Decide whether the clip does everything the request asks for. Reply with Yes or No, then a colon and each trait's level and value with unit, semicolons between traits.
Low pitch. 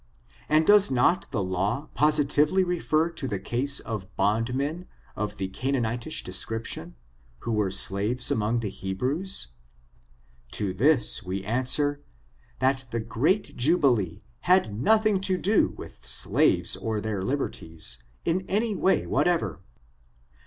Yes: low, 125 Hz